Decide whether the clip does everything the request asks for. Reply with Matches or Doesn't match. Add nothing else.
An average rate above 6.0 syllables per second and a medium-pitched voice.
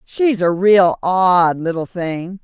Doesn't match